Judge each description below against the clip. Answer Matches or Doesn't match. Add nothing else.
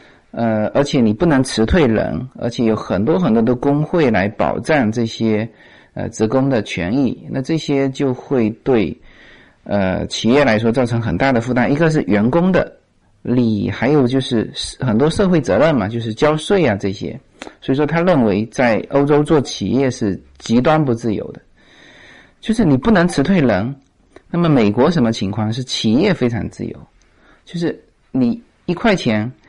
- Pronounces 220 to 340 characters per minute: Matches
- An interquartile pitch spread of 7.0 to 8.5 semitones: Doesn't match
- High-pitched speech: Doesn't match